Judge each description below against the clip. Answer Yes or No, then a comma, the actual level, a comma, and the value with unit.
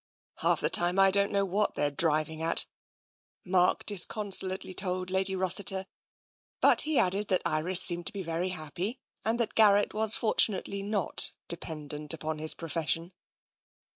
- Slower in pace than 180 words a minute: Yes, average, 160 wpm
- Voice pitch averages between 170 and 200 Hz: Yes, medium, 185 Hz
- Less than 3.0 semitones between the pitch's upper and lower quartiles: No, average, 3.3 semitones